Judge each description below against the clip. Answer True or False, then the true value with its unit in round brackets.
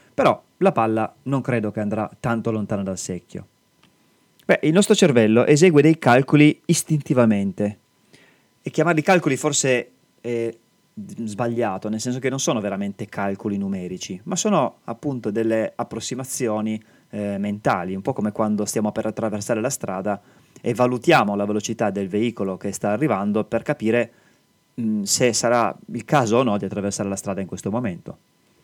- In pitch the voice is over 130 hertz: False (115 Hz)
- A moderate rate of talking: True (155 wpm)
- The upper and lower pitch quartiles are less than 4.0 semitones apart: False (4.7 semitones)